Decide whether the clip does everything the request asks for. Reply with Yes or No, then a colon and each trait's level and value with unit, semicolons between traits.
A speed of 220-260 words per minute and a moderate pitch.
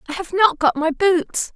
No: fast, 230 wpm; very high, 345 Hz